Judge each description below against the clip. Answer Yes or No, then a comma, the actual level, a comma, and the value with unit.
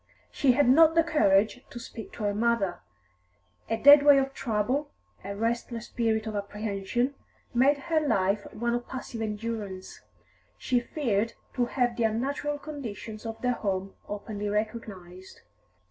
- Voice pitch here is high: Yes, high, 230 Hz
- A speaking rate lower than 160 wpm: Yes, average, 145 wpm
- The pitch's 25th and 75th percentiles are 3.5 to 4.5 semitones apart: Yes, average, 4.0 semitones